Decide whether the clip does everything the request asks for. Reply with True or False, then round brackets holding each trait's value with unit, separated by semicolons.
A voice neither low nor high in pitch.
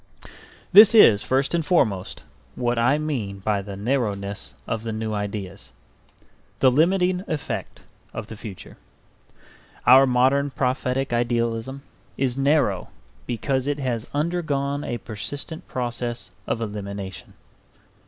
False (125 Hz)